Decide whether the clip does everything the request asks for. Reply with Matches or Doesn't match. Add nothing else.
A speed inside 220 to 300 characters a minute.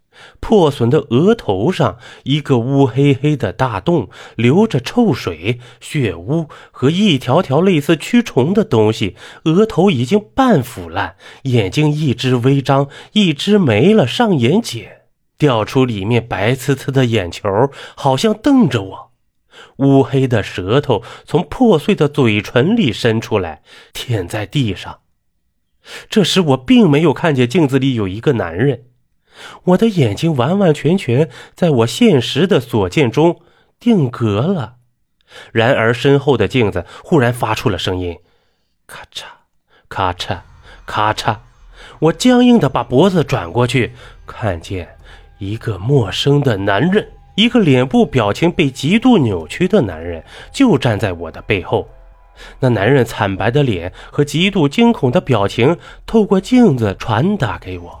Doesn't match